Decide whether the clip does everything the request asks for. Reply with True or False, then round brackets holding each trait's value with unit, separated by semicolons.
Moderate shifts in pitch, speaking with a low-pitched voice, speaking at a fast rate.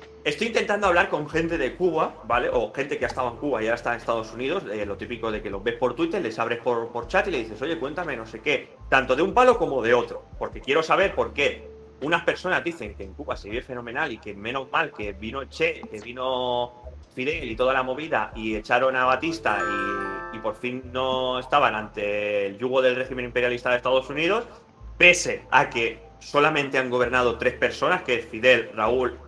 True (4.0 semitones; 125 Hz; 225 wpm)